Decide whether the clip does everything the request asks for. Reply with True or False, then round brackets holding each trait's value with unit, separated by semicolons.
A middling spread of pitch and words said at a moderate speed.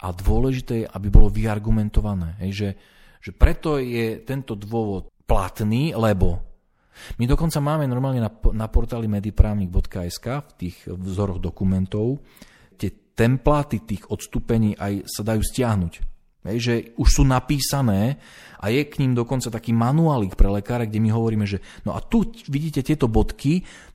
True (4.3 semitones; 140 wpm)